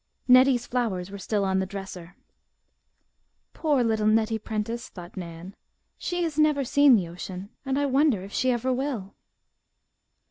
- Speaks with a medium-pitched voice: No, high, 220 Hz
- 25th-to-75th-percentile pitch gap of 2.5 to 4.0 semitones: No, wide, 5.6 semitones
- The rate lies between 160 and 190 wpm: No, average, 150 wpm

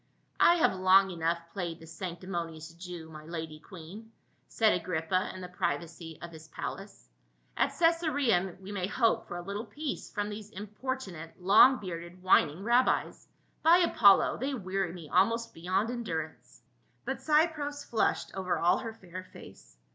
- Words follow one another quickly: No, average, 165 wpm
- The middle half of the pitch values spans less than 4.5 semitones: No, average, 5.0 semitones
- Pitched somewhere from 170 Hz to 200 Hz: Yes, medium, 185 Hz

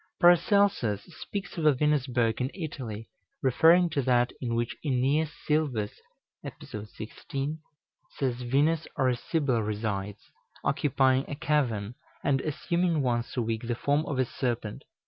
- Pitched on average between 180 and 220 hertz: No, low, 130 Hz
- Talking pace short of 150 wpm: Yes, average, 140 wpm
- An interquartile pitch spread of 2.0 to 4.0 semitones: No, average, 4.4 semitones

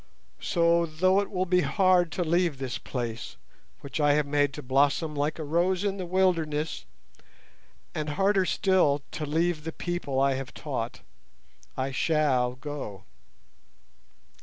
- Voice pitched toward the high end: No, medium, 155 Hz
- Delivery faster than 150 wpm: No, average, 145 wpm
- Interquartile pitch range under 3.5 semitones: No, average, 4.1 semitones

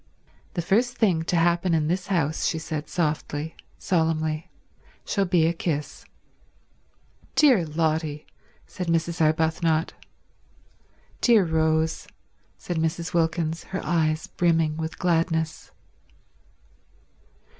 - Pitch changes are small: Yes, narrow, 1.6 semitones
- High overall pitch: No, medium, 165 Hz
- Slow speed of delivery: Yes, slow, 105 wpm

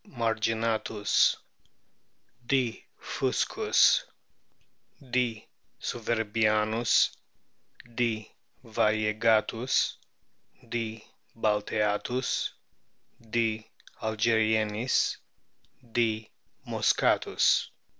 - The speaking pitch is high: No, low, 110 Hz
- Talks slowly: Yes, slow, 50 wpm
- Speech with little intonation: Yes, narrow, 1.3 semitones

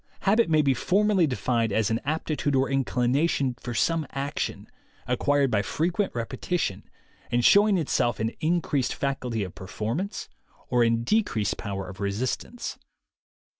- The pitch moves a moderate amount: No, wide, 6.0 semitones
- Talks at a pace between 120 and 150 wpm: Yes, slow, 135 wpm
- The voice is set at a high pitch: No, low, 130 Hz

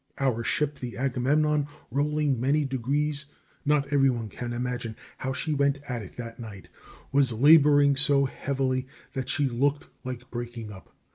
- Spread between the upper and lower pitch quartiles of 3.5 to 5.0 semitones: No, average, 2.9 semitones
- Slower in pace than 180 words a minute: Yes, average, 155 wpm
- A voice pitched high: No, low, 135 Hz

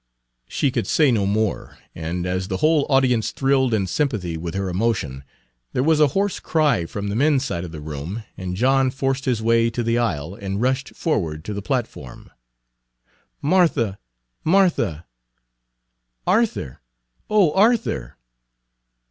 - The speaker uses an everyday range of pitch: No, wide, 7.2 semitones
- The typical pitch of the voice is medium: No, low, 115 Hz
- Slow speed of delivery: No, average, 150 wpm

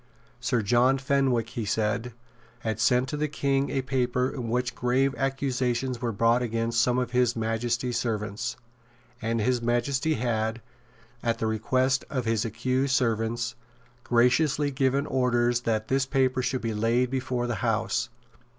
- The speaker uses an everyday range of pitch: No, narrow, 2.2 semitones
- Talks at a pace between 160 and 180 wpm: No, average, 150 wpm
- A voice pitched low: Yes, low, 125 Hz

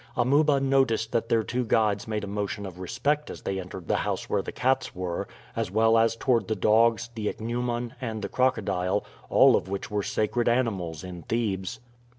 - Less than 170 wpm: No, average, 190 wpm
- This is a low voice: Yes, low, 110 Hz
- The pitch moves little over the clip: No, average, 3.4 semitones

